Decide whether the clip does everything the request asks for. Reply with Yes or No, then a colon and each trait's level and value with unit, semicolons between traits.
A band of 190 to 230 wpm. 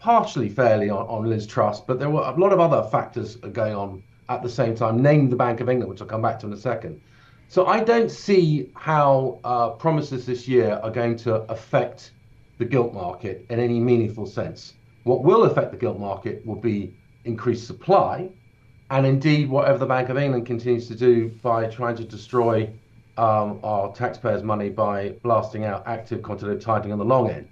Yes: average, 200 wpm